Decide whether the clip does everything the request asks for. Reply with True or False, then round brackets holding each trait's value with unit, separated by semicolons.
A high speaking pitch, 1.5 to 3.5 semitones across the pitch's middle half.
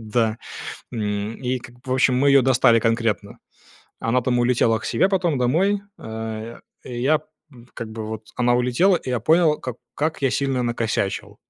False (120 Hz; 3.0 semitones)